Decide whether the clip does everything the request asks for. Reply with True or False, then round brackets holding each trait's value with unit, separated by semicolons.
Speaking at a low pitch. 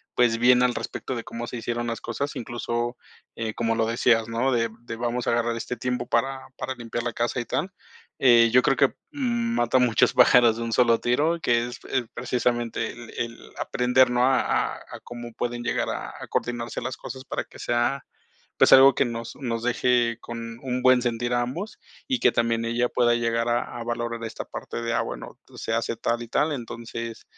True (120 Hz)